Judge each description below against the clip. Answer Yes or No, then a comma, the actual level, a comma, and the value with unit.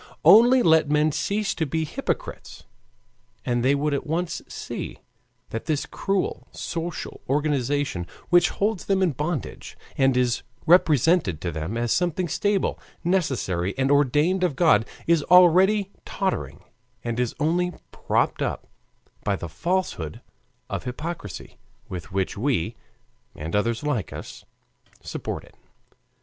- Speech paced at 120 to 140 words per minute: Yes, slow, 135 wpm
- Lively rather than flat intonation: Yes, wide, 6.8 semitones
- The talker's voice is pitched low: No, medium, 150 Hz